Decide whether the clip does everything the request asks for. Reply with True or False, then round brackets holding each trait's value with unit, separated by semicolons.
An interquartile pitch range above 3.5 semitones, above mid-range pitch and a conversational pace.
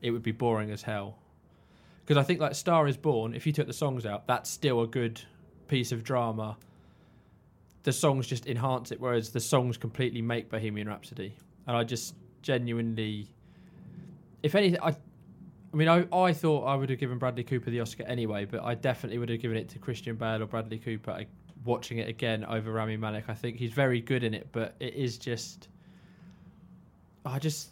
False (4.1 semitones; 120 Hz; 195 wpm)